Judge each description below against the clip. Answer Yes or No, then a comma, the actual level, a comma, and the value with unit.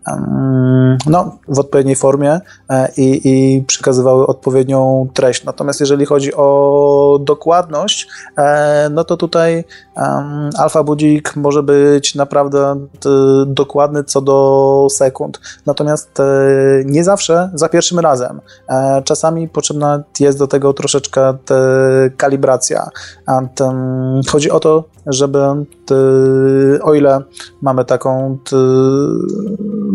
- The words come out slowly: Yes, slow, 90 wpm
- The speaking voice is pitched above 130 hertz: Yes, medium, 140 Hz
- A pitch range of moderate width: No, narrow, 1.8 semitones